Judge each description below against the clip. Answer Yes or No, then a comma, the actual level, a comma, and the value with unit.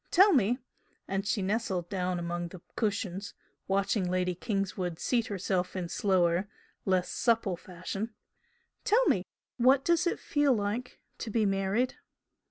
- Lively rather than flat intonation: No, average, 4.1 semitones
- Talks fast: No, average, 140 wpm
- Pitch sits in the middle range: No, high, 195 Hz